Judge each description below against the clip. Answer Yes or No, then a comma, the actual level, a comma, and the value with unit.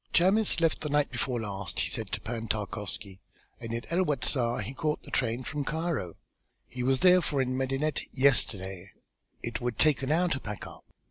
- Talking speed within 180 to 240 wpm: Yes, average, 190 wpm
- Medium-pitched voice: No, low, 130 Hz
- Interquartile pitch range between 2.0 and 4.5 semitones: No, average, 5.2 semitones